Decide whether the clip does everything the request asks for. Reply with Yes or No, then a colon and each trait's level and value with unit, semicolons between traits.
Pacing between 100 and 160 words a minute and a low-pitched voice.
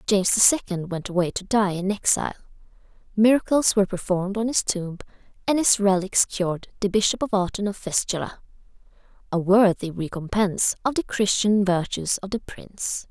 No: average, 155 wpm; high, 200 Hz